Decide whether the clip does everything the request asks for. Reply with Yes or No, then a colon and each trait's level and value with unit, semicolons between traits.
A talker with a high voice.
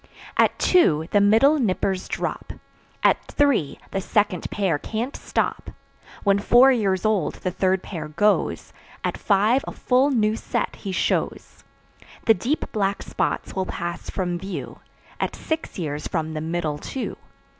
Yes: high, 195 Hz